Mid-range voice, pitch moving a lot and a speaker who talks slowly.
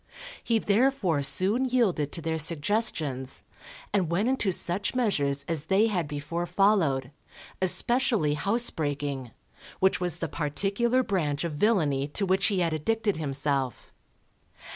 Yes: medium, 175 Hz; wide, 6.3 semitones; slow, 130 wpm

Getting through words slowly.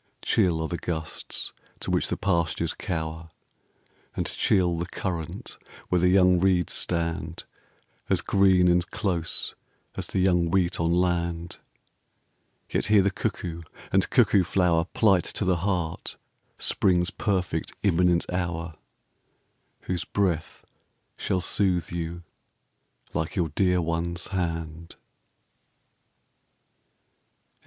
Yes: slow, 115 wpm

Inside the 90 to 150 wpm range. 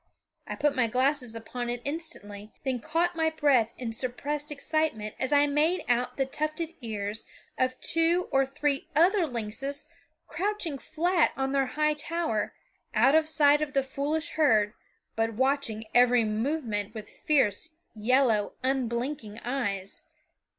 Yes: average, 145 wpm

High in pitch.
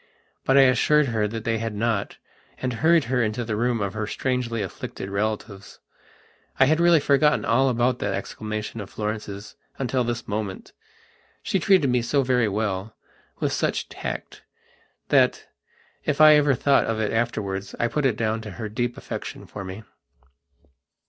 No: low, 115 Hz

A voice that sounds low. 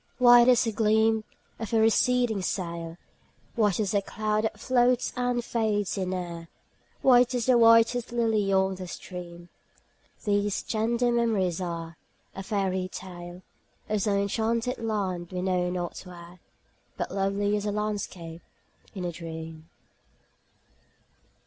No: high, 205 Hz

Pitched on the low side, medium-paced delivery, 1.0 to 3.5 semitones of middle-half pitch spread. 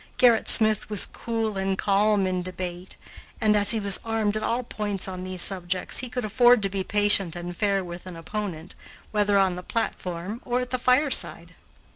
No: high, 205 Hz; average, 190 wpm; average, 3.2 semitones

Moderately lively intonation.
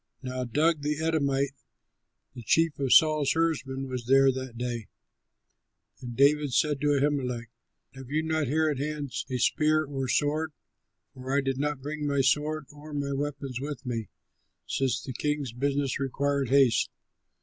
No: narrow, 2.2 semitones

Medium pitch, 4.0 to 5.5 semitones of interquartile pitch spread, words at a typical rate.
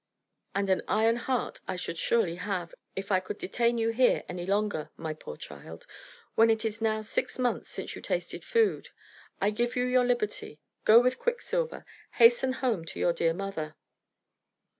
No: high, 220 Hz; average, 4.8 semitones; average, 175 wpm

